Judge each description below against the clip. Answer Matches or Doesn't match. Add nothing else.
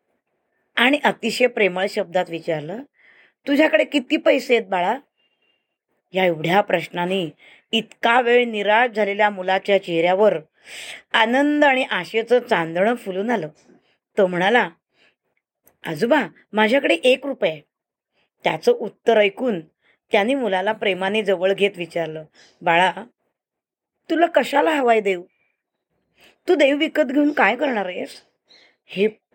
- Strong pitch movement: Matches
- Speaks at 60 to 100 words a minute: Doesn't match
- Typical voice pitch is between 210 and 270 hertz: Matches